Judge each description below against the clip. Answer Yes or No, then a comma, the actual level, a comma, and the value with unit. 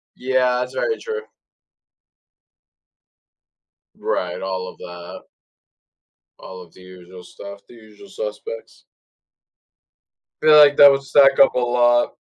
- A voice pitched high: No, low, 125 Hz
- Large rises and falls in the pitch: Yes, wide, 7.4 semitones